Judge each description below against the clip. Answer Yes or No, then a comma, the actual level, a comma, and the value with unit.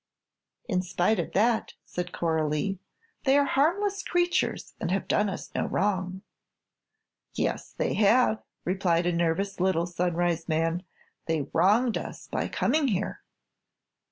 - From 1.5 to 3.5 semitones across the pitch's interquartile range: No, average, 4.7 semitones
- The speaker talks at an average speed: No, slow, 130 wpm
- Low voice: No, high, 190 Hz